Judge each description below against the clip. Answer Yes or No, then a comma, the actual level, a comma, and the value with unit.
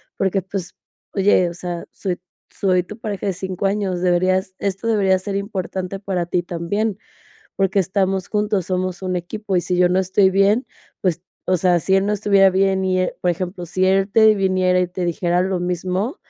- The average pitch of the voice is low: No, high, 190 Hz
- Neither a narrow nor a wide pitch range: No, narrow, 1.6 semitones